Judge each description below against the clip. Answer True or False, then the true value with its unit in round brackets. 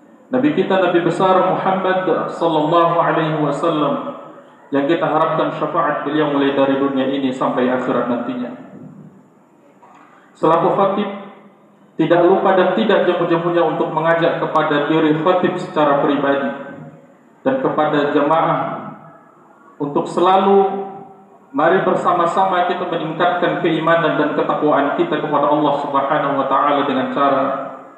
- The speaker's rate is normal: True (120 wpm)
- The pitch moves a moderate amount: True (3.9 semitones)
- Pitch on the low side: False (165 Hz)